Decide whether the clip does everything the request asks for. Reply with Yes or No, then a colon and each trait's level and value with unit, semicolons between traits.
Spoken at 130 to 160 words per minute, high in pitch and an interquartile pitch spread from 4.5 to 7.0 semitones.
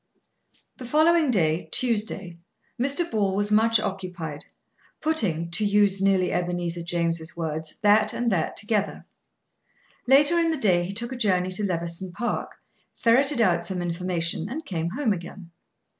Yes: average, 145 wpm; high, 195 Hz; average, 5.2 semitones